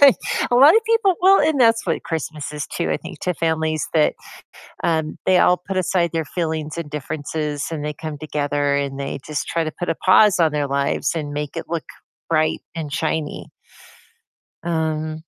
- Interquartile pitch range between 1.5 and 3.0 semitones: Yes, narrow, 2.6 semitones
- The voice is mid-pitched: Yes, medium, 160 Hz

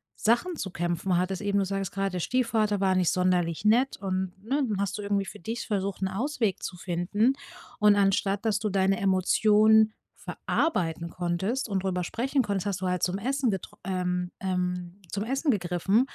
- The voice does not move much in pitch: No, average, 3.0 semitones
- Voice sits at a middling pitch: No, high, 195 Hz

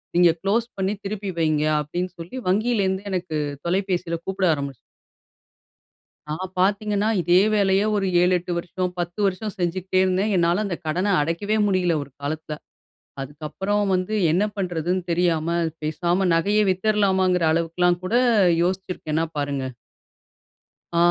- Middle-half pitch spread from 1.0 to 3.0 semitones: Yes, average, 2.7 semitones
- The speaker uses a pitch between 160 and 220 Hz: Yes, medium, 185 Hz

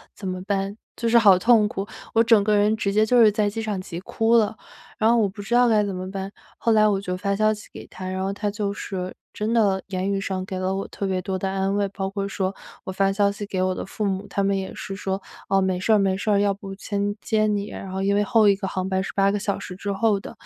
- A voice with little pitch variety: Yes, narrow, 1.7 semitones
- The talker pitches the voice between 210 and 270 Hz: No, high, 200 Hz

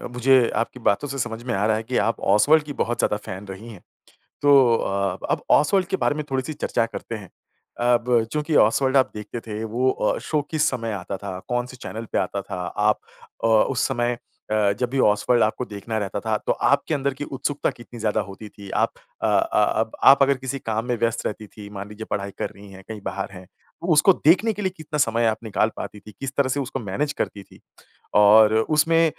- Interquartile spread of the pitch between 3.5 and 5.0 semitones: Yes, average, 4.6 semitones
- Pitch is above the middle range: No, low, 115 Hz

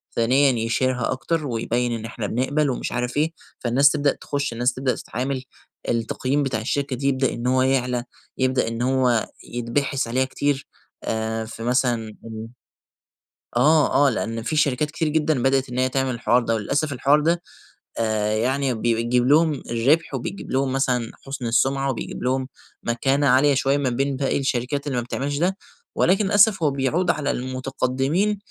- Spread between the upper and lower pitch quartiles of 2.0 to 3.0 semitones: Yes, average, 2.7 semitones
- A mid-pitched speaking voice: No, low, 130 Hz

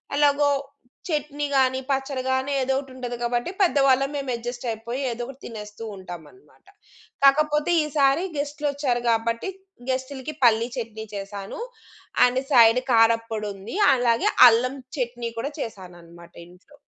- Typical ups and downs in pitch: Yes, average, 3.5 semitones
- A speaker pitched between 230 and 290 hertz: Yes, very high, 250 Hz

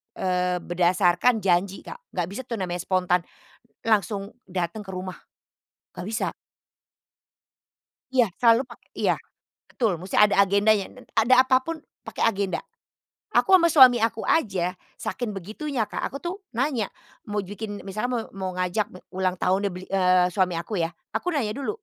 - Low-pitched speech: No, high, 200 Hz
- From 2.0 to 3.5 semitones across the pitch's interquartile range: No, average, 4.0 semitones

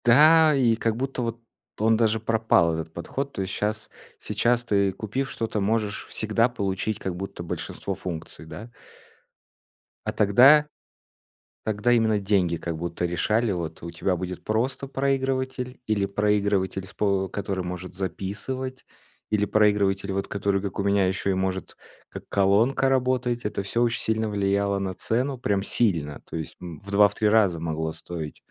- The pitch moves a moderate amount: Yes, average, 3.6 semitones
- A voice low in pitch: Yes, low, 105 Hz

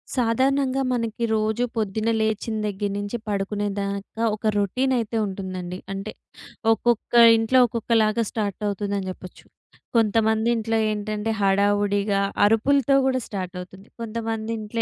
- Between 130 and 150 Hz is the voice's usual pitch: No, high, 215 Hz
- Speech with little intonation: Yes, narrow, 2.2 semitones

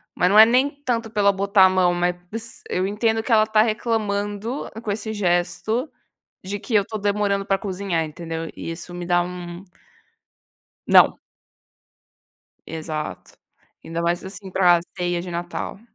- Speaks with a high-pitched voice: Yes, high, 195 Hz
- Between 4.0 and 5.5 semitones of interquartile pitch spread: No, average, 3.4 semitones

